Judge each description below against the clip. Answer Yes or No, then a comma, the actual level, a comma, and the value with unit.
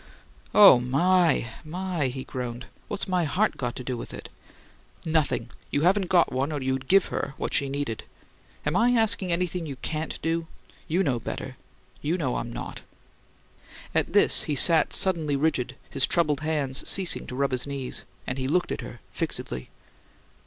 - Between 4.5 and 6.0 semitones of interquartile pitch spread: Yes, average, 5.2 semitones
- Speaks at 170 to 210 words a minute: Yes, average, 175 wpm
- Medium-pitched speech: Yes, medium, 150 Hz